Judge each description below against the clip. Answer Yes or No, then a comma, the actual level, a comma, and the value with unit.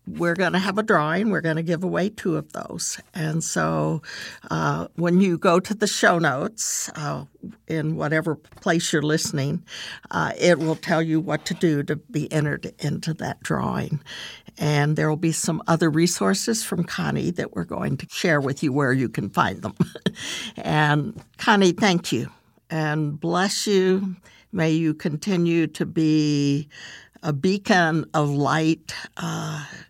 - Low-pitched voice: No, medium, 160 Hz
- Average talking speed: Yes, average, 165 wpm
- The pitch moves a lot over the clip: No, average, 2.9 semitones